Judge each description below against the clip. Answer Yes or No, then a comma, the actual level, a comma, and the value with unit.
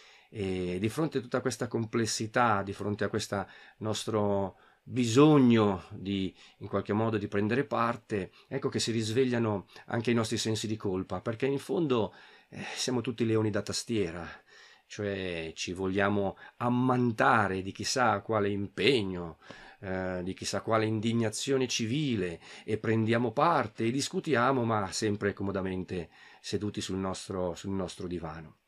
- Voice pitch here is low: Yes, low, 110 Hz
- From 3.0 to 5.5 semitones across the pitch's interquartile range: Yes, average, 3.4 semitones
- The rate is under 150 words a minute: Yes, average, 140 wpm